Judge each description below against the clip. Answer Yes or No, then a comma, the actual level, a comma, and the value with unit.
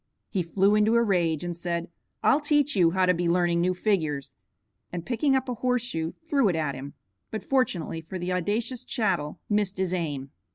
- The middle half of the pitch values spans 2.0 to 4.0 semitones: No, average, 5.2 semitones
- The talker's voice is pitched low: No, medium, 185 Hz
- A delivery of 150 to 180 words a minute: No, average, 200 wpm